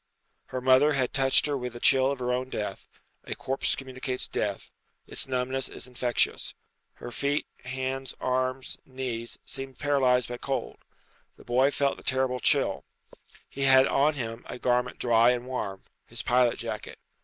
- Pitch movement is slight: Yes, narrow, 1.4 semitones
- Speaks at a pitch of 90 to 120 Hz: No, low, 130 Hz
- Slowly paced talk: No, average, 165 wpm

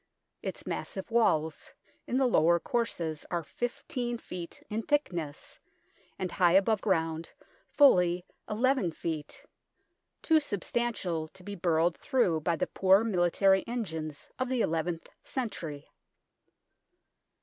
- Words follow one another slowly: Yes, slow, 120 wpm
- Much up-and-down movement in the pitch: Yes, wide, 6.2 semitones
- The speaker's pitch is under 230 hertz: Yes, medium, 185 Hz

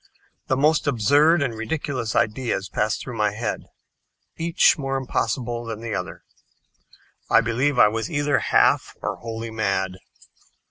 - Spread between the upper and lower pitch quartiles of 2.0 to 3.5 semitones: No, average, 4.3 semitones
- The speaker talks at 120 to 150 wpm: Yes, average, 140 wpm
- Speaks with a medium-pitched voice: No, low, 120 Hz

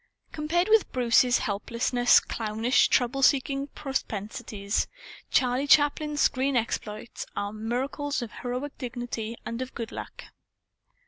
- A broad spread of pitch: No, average, 3.4 semitones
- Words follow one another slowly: Yes, slow, 115 wpm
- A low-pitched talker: No, very high, 250 Hz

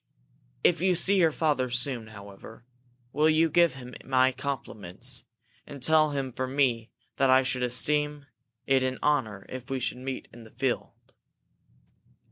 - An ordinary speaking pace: Yes, average, 155 wpm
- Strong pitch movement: No, average, 3.1 semitones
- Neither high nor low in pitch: No, low, 130 Hz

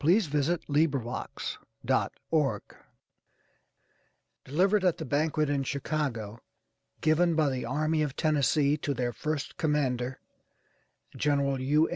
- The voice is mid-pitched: Yes, medium, 145 Hz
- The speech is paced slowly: Yes, slow, 115 wpm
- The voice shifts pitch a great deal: No, narrow, 2.6 semitones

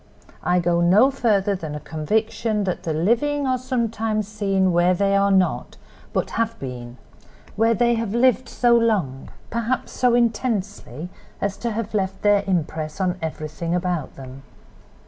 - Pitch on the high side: Yes, high, 200 Hz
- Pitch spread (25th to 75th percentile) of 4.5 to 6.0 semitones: Yes, average, 5.0 semitones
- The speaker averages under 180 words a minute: Yes, average, 150 wpm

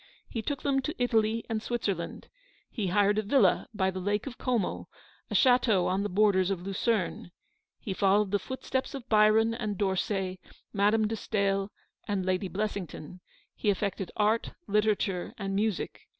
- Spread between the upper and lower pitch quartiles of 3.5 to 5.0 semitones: No, narrow, 2.5 semitones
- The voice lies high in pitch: Yes, high, 205 Hz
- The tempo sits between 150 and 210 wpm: Yes, average, 160 wpm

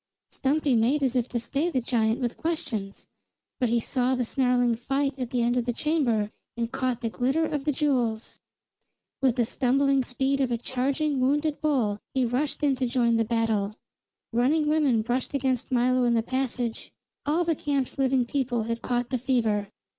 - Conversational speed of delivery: Yes, average, 180 wpm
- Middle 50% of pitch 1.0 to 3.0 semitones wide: Yes, average, 2.7 semitones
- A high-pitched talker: Yes, very high, 255 Hz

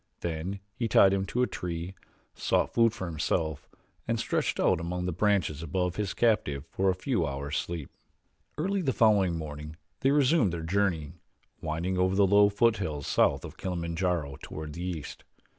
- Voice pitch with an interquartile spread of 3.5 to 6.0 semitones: Yes, average, 4.2 semitones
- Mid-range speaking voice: No, very low, 90 Hz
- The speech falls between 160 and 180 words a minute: Yes, average, 170 wpm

